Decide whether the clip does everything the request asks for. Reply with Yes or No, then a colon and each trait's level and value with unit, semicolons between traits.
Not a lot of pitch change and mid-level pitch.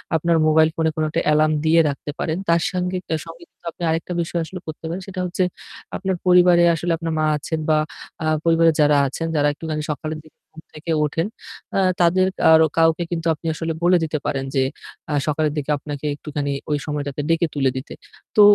Yes: narrow, 2.0 semitones; medium, 160 Hz